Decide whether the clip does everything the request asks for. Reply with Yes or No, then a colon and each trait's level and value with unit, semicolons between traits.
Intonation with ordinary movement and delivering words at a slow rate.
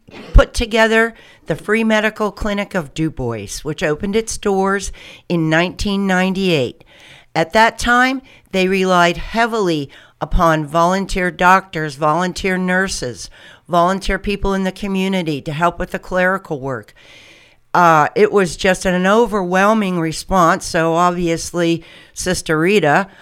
Yes: average, 3.2 semitones; slow, 130 wpm